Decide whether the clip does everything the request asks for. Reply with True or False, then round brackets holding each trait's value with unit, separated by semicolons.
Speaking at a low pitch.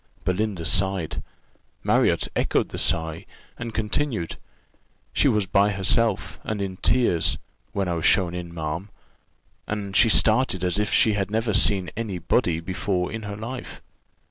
True (100 Hz)